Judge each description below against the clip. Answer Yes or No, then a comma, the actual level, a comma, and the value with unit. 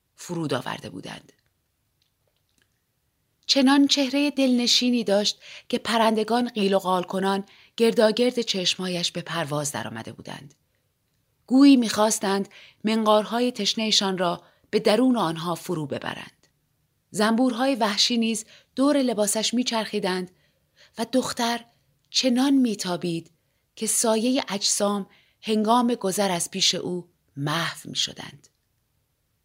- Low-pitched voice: No, high, 210 Hz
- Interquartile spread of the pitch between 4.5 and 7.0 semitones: Yes, average, 5.1 semitones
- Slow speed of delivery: Yes, slow, 100 wpm